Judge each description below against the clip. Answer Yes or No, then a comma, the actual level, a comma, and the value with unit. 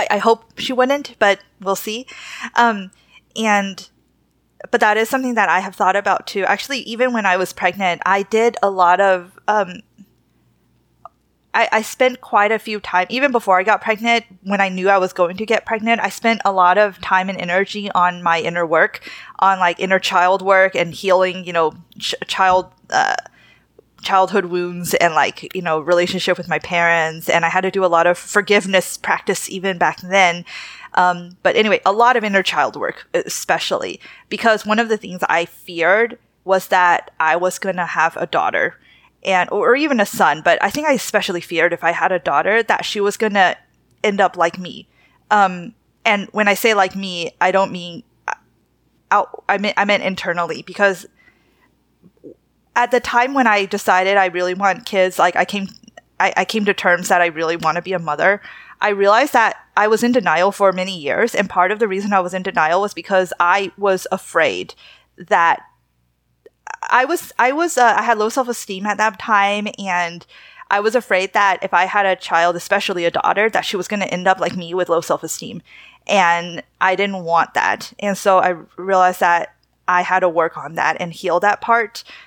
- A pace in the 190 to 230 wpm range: Yes, fast, 205 wpm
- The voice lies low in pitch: No, high, 190 Hz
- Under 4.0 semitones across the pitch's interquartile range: Yes, average, 2.9 semitones